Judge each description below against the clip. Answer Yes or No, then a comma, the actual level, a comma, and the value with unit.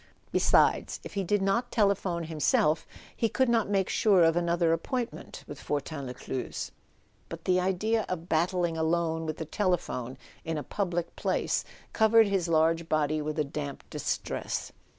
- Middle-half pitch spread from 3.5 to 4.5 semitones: Yes, average, 3.8 semitones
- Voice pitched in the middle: Yes, medium, 170 Hz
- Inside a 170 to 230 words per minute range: No, average, 160 wpm